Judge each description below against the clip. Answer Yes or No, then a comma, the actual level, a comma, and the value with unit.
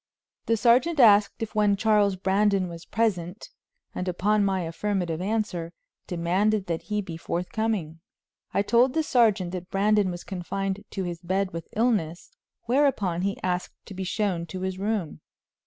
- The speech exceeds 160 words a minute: No, average, 155 wpm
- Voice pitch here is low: No, high, 195 Hz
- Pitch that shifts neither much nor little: Yes, average, 3.1 semitones